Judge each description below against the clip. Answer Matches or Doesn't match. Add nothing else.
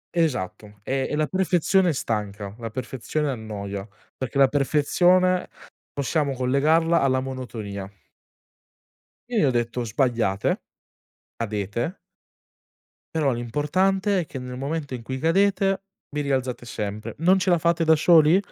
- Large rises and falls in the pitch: Matches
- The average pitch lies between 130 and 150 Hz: Matches